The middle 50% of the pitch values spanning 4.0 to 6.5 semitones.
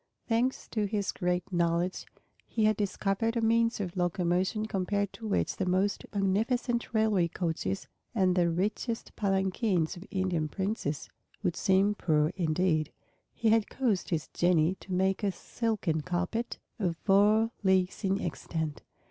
No: average, 3.4 semitones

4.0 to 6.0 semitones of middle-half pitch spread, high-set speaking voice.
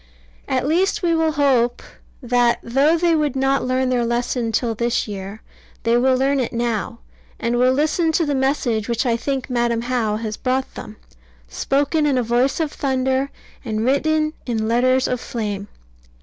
No: average, 3.0 semitones; very high, 255 Hz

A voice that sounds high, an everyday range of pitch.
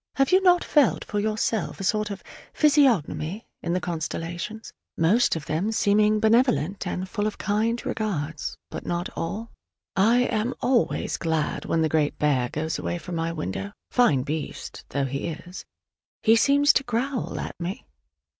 No: high, 200 Hz; wide, 6.0 semitones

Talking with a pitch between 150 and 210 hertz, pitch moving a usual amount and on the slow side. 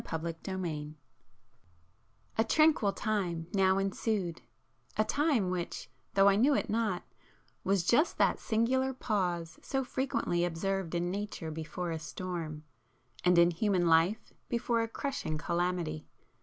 Yes: medium, 185 Hz; average, 4.5 semitones; slow, 130 wpm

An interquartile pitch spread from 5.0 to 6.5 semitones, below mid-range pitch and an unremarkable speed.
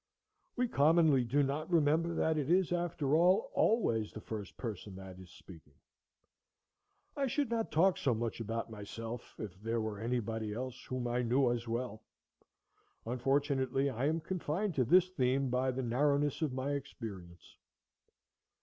Yes: wide, 5.5 semitones; low, 130 Hz; average, 155 wpm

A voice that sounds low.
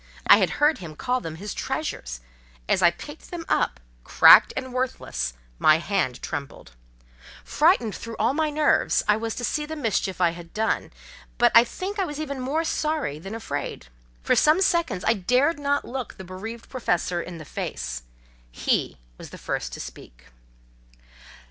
No: high, 230 Hz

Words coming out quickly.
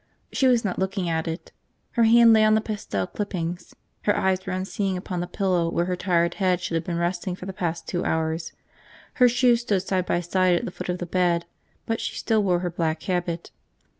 Yes: fast, 225 wpm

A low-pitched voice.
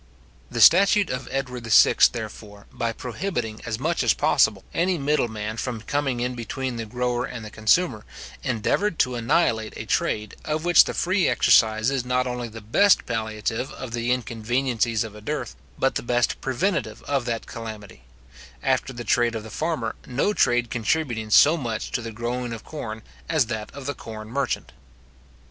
Yes: low, 120 Hz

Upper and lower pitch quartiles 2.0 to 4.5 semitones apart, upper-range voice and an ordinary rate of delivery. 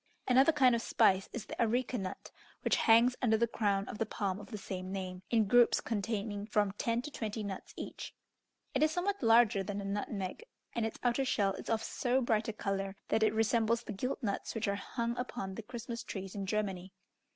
No: average, 3.1 semitones; high, 220 Hz; fast, 210 wpm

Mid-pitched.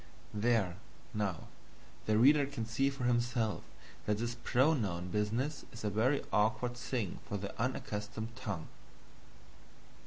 No: low, 115 Hz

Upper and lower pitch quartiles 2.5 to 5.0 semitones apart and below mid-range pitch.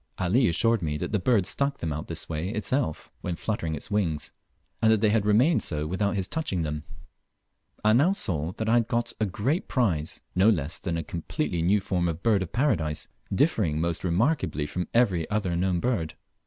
No: wide, 5.6 semitones; very low, 95 Hz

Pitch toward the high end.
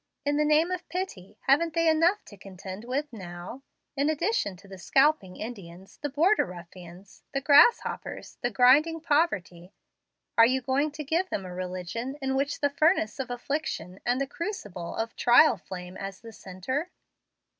Yes: very high, 255 Hz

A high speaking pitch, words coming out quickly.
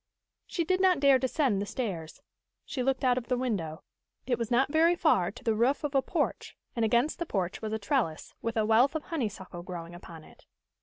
Yes: high, 240 Hz; fast, 215 wpm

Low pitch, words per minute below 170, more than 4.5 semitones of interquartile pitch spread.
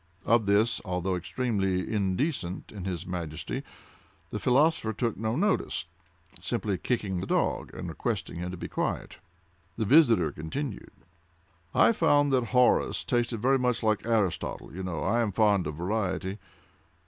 Yes: low, 105 Hz; average, 140 wpm; average, 5.1 semitones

